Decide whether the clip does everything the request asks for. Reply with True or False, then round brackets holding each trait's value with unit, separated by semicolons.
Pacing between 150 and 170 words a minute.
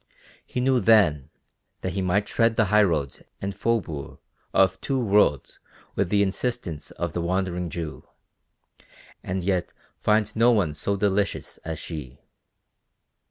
False (135 wpm)